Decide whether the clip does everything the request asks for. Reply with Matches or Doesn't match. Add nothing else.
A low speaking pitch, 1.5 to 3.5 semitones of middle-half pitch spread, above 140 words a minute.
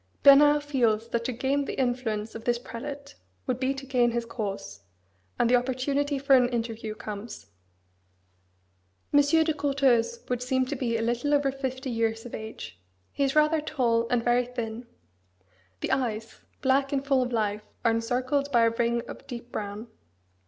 Doesn't match